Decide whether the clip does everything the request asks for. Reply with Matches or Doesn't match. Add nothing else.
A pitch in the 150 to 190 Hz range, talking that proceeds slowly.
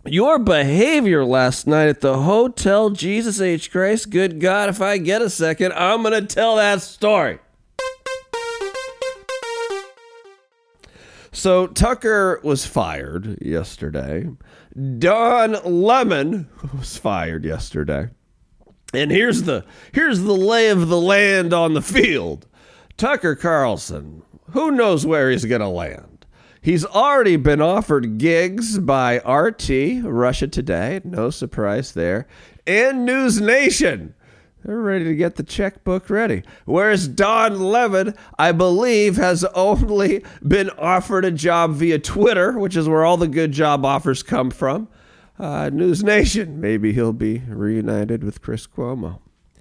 Matches